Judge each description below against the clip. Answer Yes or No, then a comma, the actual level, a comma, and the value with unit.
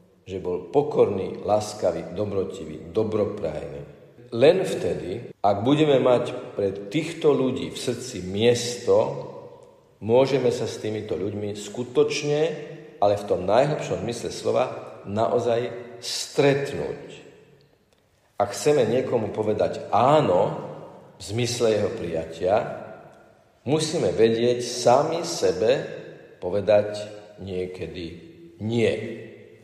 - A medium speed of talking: No, slow, 95 wpm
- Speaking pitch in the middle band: No, low, 120 Hz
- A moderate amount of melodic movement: No, wide, 6.3 semitones